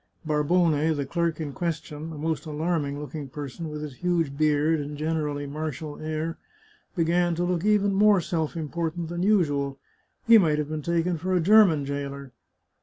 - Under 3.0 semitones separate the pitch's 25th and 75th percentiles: Yes, narrow, 2.6 semitones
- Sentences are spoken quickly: No, average, 170 wpm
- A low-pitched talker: No, medium, 160 Hz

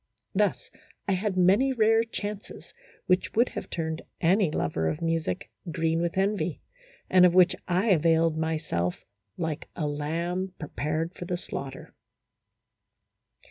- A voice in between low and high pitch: Yes, medium, 170 Hz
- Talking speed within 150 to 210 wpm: No, slow, 135 wpm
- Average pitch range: Yes, average, 3.0 semitones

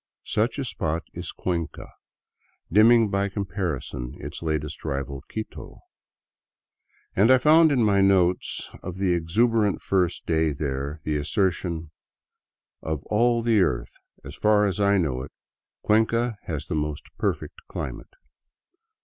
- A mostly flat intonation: No, wide, 5.6 semitones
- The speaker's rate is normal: No, slow, 130 wpm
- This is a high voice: No, very low, 90 Hz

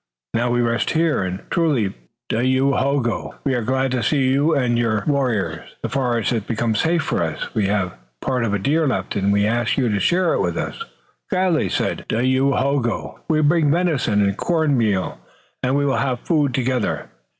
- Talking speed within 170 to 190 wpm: Yes, average, 185 wpm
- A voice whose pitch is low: Yes, low, 130 Hz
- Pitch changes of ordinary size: Yes, average, 4.3 semitones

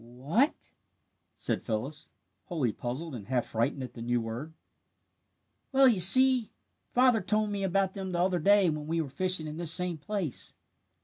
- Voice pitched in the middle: Yes, medium, 170 Hz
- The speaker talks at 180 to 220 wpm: Yes, average, 190 wpm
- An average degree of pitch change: No, wide, 7.3 semitones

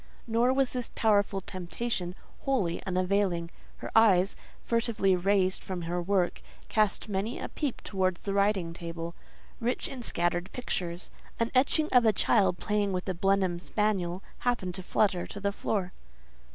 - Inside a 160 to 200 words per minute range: No, average, 150 wpm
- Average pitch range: Yes, average, 3.8 semitones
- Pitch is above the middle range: Yes, high, 195 Hz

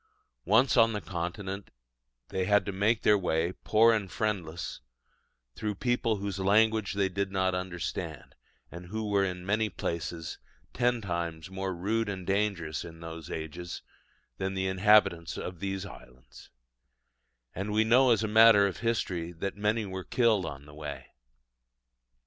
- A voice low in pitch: Yes, very low, 95 Hz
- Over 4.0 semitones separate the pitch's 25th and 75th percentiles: No, average, 3.5 semitones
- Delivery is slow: No, average, 155 wpm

